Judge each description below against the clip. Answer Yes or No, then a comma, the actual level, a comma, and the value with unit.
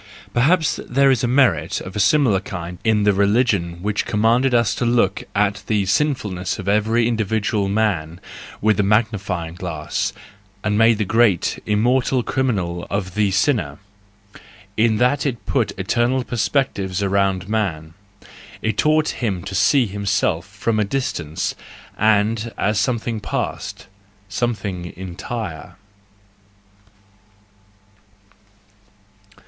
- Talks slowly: Yes, slow, 130 wpm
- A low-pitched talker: Yes, low, 105 Hz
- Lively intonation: No, average, 3.7 semitones